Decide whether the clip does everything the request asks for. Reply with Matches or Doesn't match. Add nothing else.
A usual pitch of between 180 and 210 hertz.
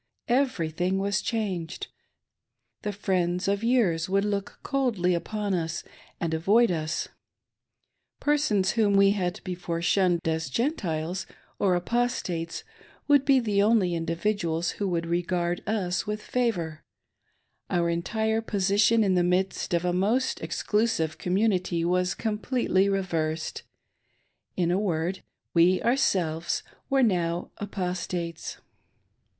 Matches